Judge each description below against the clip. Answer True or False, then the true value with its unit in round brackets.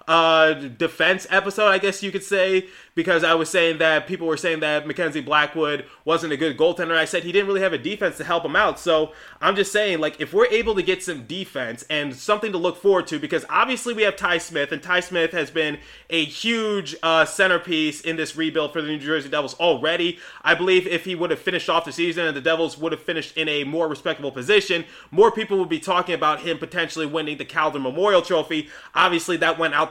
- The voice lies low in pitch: False (165 Hz)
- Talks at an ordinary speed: False (230 wpm)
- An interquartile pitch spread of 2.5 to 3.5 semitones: True (2.8 semitones)